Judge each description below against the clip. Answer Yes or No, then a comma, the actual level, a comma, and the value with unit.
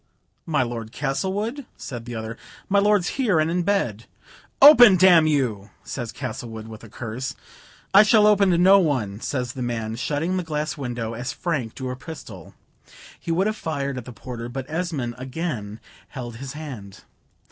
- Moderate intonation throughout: No, wide, 6.9 semitones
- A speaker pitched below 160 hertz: Yes, low, 135 Hz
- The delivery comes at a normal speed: Yes, average, 180 wpm